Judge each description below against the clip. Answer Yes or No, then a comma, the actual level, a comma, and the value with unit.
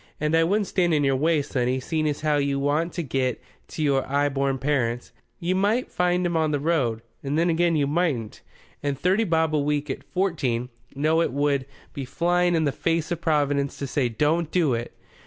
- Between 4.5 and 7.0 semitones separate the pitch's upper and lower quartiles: No, average, 3.4 semitones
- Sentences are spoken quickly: Yes, fast, 210 wpm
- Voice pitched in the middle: Yes, medium, 150 Hz